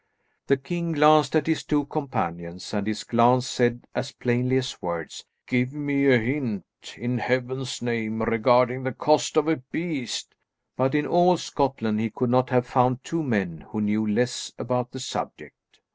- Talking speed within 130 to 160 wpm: No, average, 170 wpm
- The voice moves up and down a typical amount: Yes, average, 3.4 semitones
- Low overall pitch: Yes, low, 125 Hz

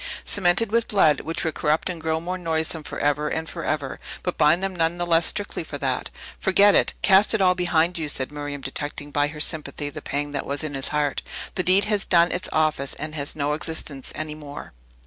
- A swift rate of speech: Yes, fast, 215 wpm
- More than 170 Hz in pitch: No, medium, 160 Hz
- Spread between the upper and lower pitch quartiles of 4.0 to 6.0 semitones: No, average, 3.3 semitones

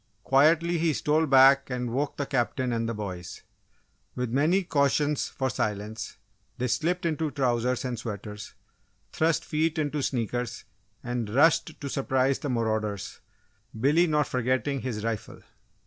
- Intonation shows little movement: No, average, 4.4 semitones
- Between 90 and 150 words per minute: Yes, average, 140 wpm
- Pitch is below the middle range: Yes, low, 130 Hz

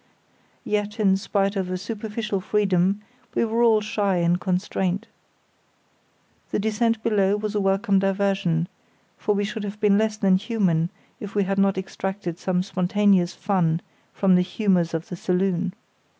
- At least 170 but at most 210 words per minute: No, average, 155 wpm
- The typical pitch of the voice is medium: No, high, 195 Hz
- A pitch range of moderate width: No, narrow, 2.2 semitones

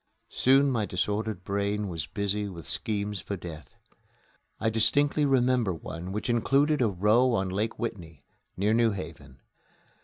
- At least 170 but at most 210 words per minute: No, average, 145 wpm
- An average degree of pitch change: Yes, average, 4.2 semitones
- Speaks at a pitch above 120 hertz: No, low, 105 Hz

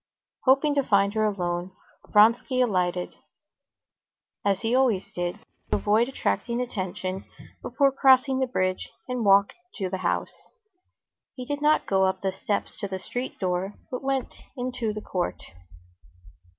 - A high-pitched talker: Yes, high, 210 Hz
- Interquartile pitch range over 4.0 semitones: Yes, average, 5.2 semitones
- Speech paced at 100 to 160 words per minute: Yes, average, 145 wpm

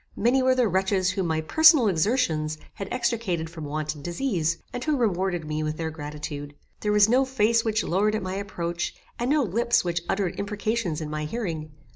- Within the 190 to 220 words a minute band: Yes, average, 195 wpm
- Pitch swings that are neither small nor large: No, wide, 6.4 semitones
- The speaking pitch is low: No, high, 190 Hz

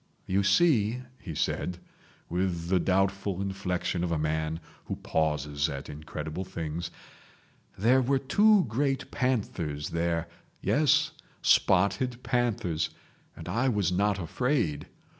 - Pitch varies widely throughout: Yes, wide, 6.4 semitones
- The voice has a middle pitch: No, very low, 95 Hz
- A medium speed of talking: No, slow, 120 wpm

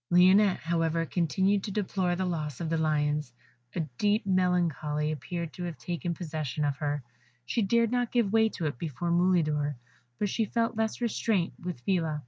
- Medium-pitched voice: Yes, medium, 175 Hz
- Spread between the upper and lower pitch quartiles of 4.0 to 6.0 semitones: Yes, average, 4.3 semitones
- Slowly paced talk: No, average, 175 wpm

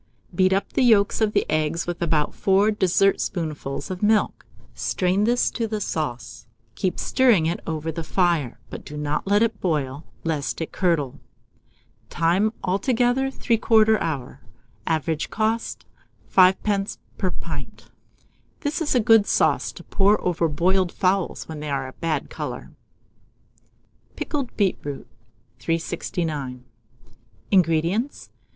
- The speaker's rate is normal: No, slow, 130 wpm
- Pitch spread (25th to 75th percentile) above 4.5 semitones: Yes, average, 5.0 semitones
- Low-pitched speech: No, medium, 180 Hz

